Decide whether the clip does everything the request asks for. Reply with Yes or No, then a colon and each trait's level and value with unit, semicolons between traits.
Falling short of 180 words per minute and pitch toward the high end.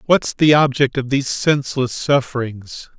No: average, 140 wpm; low, 135 Hz